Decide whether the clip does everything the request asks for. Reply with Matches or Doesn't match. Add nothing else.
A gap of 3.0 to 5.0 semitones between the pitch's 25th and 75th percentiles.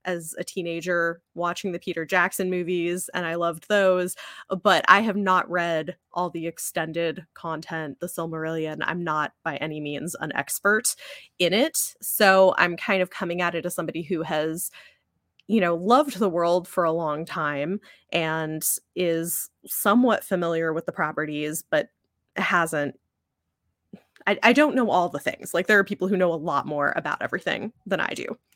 Doesn't match